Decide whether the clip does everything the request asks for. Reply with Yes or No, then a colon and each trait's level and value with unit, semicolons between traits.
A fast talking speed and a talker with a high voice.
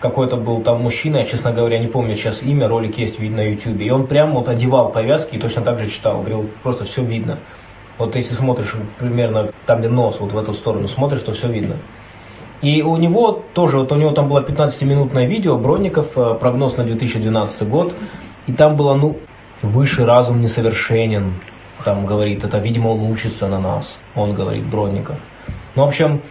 No: fast, 190 wpm; low, 115 Hz